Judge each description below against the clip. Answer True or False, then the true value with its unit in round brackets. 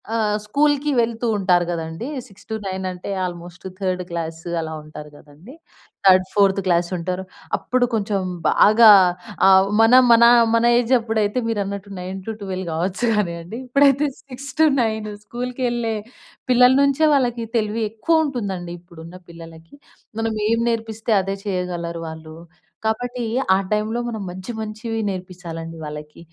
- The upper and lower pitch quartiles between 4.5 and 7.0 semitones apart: True (4.8 semitones)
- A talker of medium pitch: False (205 Hz)